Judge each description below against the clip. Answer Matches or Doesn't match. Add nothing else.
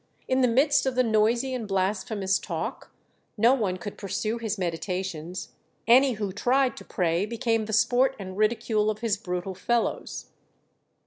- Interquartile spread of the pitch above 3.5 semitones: Matches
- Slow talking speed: Doesn't match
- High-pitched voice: Matches